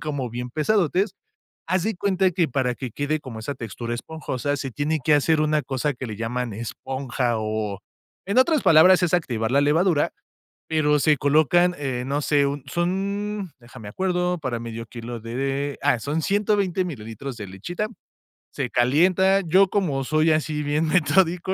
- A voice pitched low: No, medium, 145 Hz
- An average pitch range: No, wide, 6.1 semitones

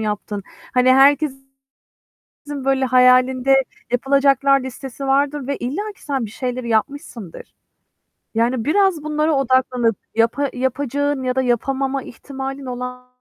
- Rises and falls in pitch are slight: Yes, narrow, 1.9 semitones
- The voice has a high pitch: Yes, very high, 265 Hz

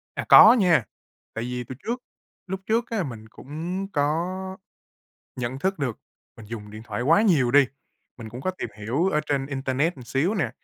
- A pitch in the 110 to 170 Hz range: Yes, medium, 140 Hz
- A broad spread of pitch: Yes, wide, 6.9 semitones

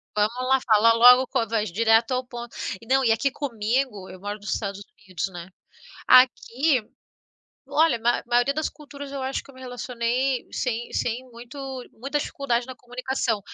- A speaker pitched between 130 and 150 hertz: No, high, 245 Hz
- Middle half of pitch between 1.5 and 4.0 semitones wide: Yes, average, 2.8 semitones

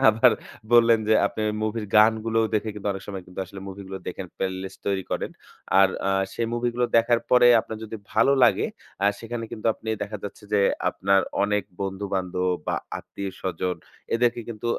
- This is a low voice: Yes, low, 105 Hz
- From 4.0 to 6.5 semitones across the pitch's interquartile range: No, average, 2.9 semitones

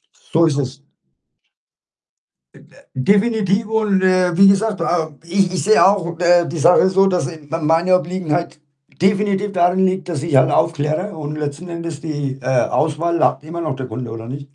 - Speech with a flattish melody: No, average, 3.8 semitones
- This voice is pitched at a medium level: Yes, medium, 170 Hz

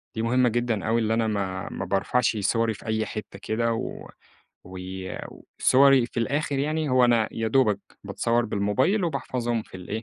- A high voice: No, low, 115 Hz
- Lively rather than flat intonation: No, average, 2.9 semitones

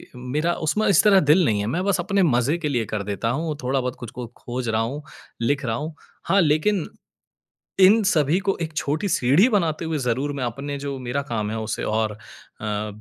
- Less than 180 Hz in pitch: Yes, medium, 140 Hz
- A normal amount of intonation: No, wide, 5.7 semitones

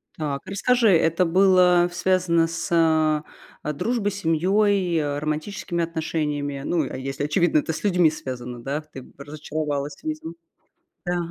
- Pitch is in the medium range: Yes, medium, 160 Hz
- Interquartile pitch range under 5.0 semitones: Yes, average, 3.3 semitones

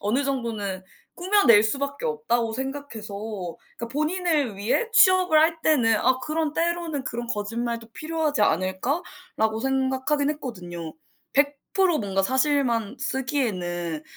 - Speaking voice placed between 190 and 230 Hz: No, very high, 265 Hz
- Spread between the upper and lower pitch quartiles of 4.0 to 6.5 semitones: Yes, wide, 5.8 semitones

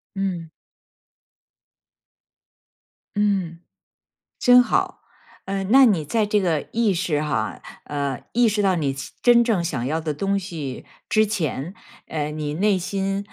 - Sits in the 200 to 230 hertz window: No, medium, 185 Hz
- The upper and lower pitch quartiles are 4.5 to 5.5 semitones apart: Yes, average, 5.2 semitones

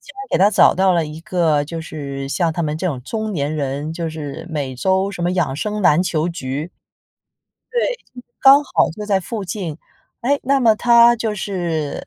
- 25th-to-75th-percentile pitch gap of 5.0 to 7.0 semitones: Yes, wide, 5.5 semitones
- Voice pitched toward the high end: No, medium, 175 Hz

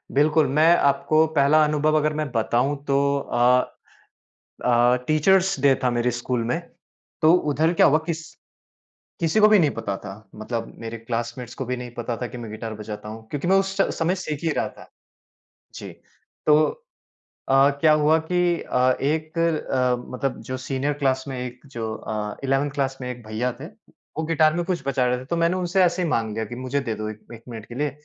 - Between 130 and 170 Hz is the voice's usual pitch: Yes, low, 135 Hz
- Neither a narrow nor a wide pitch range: Yes, average, 4.6 semitones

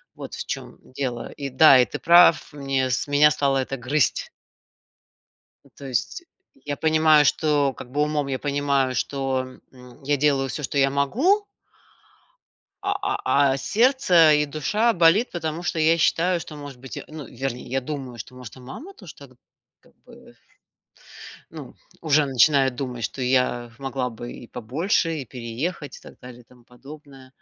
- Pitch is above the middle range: No, medium, 140 Hz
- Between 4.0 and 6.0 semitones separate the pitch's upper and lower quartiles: No, average, 3.2 semitones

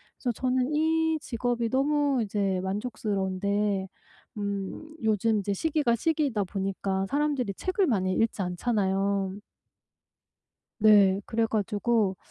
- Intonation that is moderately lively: Yes, average, 4.7 semitones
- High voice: Yes, high, 215 Hz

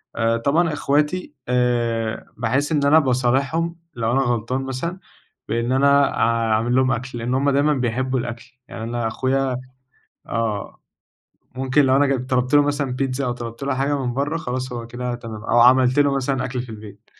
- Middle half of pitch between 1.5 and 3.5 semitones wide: Yes, average, 2.8 semitones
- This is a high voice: No, low, 130 Hz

